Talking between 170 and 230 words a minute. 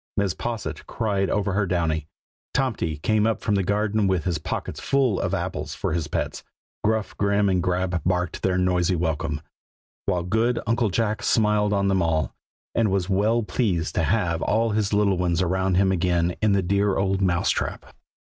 Yes: average, 185 wpm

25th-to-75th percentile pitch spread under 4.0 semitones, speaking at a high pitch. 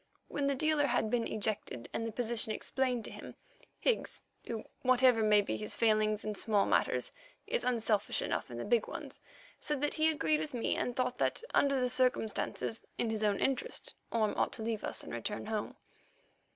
Yes: average, 3.4 semitones; high, 230 Hz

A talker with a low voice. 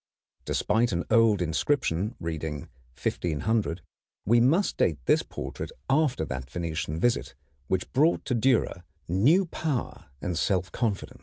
Yes: low, 105 Hz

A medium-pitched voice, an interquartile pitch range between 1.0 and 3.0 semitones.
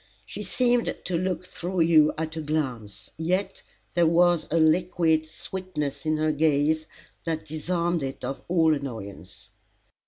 Yes: medium, 160 Hz; narrow, 2.5 semitones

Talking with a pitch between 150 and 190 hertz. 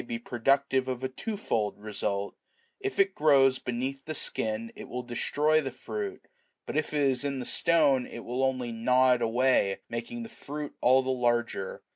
No: low, 130 Hz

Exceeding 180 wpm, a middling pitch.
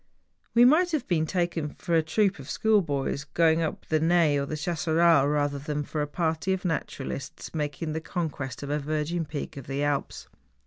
Yes: average, 195 wpm; medium, 155 Hz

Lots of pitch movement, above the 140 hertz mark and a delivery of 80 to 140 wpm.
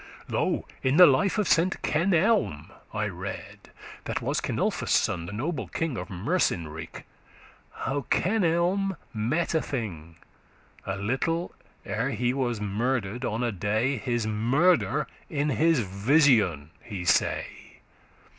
No: wide, 7.9 semitones; low, 125 Hz; slow, 135 wpm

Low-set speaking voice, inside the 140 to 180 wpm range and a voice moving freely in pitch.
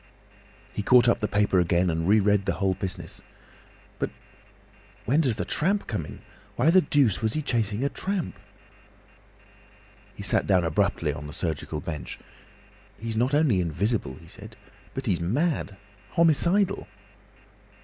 Yes: low, 105 Hz; average, 150 wpm; wide, 7.9 semitones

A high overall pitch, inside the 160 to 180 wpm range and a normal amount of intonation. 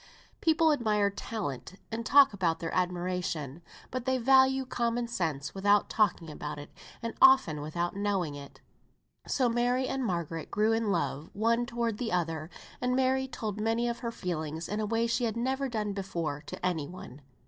No: high, 210 Hz; average, 175 wpm; wide, 5.9 semitones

